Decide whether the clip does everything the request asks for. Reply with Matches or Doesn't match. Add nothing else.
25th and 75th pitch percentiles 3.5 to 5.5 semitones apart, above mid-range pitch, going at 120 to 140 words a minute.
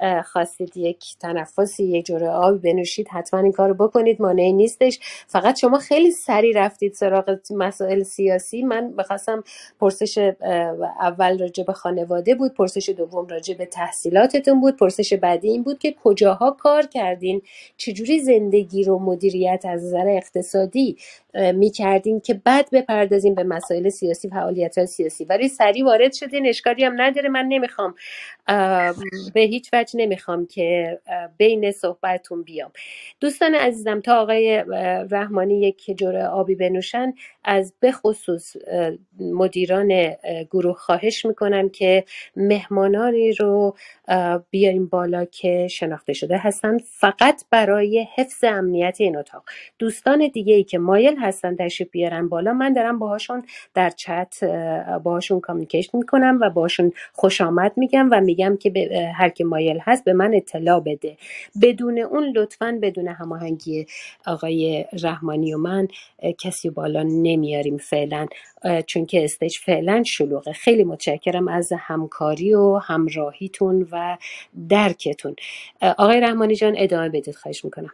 Matches